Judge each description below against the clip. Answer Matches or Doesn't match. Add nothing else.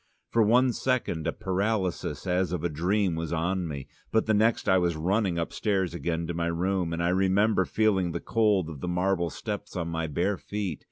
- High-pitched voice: Doesn't match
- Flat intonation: Doesn't match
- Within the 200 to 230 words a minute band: Matches